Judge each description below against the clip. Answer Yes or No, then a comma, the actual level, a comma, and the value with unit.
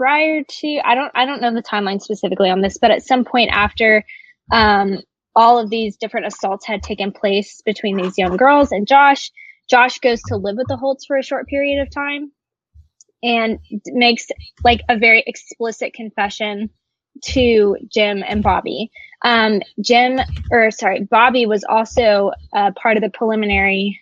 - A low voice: No, high, 225 Hz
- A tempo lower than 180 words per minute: Yes, average, 170 wpm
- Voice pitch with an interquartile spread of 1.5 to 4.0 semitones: Yes, average, 3.5 semitones